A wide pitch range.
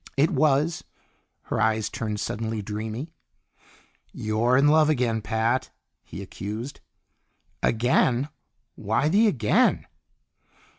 No: average, 4.5 semitones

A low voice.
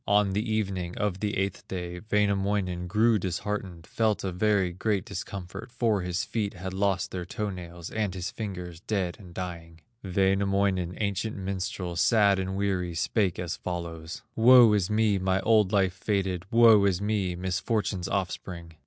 Yes: very low, 95 Hz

